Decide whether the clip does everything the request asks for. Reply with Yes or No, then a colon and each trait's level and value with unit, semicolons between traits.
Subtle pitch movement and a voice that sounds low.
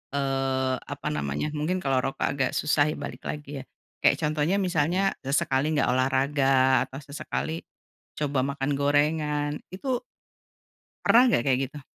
No: narrow, 2.2 semitones; medium, 145 Hz